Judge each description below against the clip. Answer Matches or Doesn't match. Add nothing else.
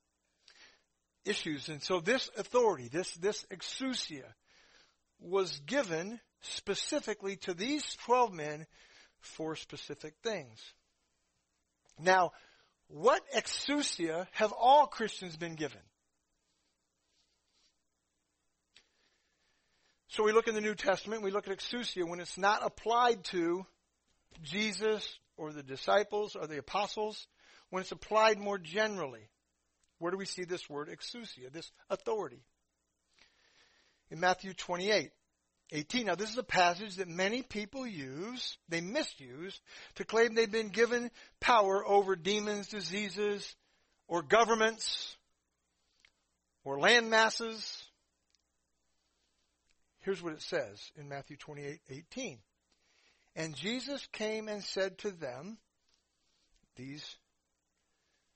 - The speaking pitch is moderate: Matches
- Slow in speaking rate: Matches